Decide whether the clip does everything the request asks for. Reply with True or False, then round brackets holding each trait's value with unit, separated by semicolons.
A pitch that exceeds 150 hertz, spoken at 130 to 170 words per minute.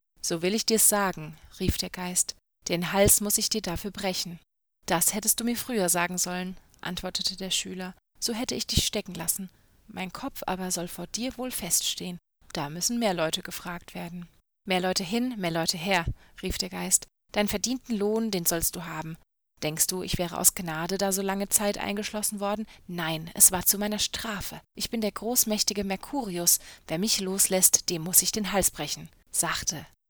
False (185 Hz; 185 wpm)